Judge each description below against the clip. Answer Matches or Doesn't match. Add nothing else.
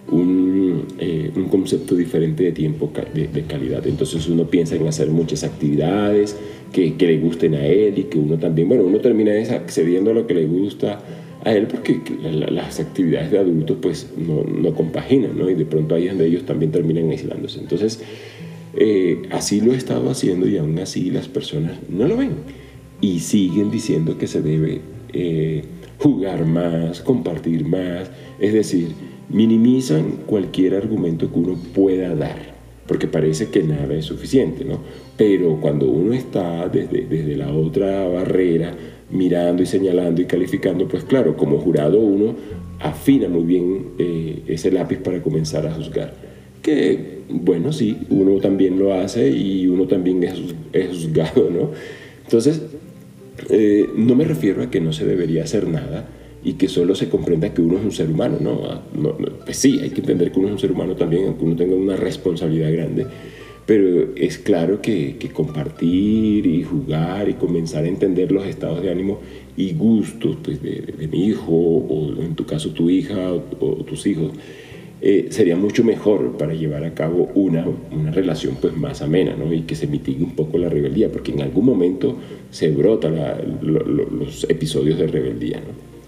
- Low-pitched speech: Matches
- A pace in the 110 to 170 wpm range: Doesn't match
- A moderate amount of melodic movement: Matches